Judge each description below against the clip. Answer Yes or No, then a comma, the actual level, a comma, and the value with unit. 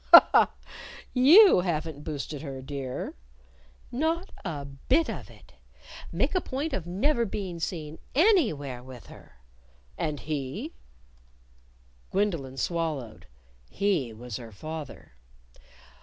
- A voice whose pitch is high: No, medium, 160 Hz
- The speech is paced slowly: Yes, slow, 110 wpm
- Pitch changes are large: Yes, wide, 7.4 semitones